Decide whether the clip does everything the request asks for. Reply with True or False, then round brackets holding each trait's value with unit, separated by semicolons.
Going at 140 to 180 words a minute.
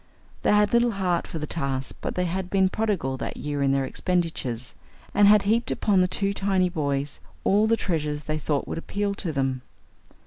False (200 wpm)